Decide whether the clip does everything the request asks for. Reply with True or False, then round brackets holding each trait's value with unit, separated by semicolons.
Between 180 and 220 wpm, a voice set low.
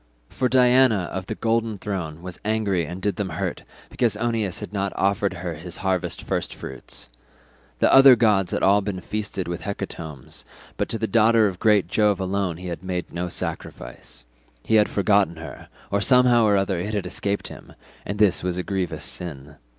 True (190 wpm; 100 Hz)